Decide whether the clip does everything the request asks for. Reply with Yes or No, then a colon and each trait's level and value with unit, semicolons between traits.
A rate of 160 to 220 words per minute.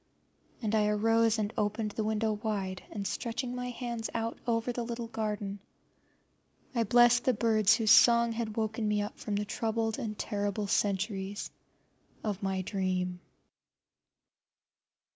No: average, 145 wpm